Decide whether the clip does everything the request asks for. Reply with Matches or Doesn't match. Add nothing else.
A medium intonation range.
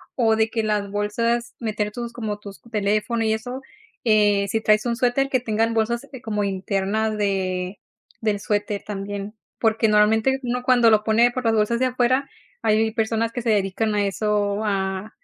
Doesn't match